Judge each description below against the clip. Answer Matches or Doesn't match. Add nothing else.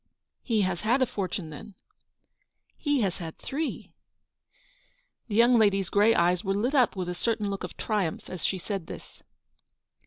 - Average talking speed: Matches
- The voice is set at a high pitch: Matches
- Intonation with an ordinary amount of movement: Matches